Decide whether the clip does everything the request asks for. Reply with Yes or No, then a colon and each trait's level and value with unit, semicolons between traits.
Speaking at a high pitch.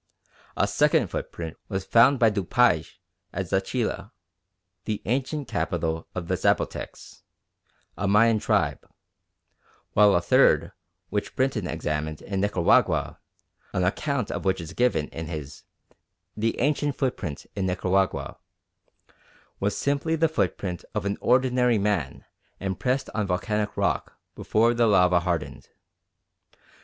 No: low, 100 Hz